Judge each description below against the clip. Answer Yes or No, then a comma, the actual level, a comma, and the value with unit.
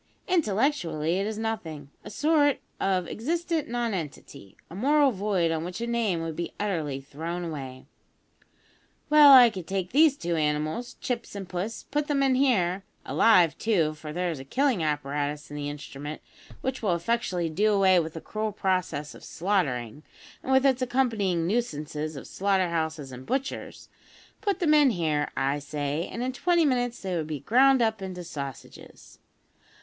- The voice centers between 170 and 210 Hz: Yes, medium, 185 Hz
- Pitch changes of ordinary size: No, wide, 7.7 semitones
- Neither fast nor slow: Yes, average, 170 wpm